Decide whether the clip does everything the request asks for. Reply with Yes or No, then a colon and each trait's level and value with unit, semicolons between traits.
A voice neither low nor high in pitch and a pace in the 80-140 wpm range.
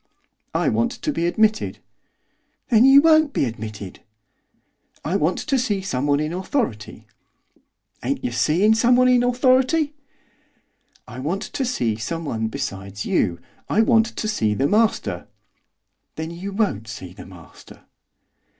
Yes: medium, 180 Hz; slow, 135 wpm